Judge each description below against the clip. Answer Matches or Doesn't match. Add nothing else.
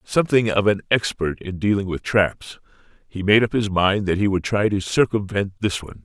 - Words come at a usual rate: Doesn't match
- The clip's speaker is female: Doesn't match